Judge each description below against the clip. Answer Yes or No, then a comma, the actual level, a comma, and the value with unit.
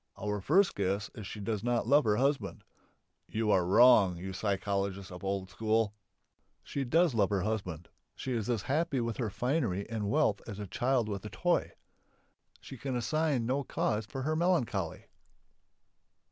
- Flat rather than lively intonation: No, average, 4.9 semitones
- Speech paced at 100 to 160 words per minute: No, average, 175 wpm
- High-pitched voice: No, low, 110 Hz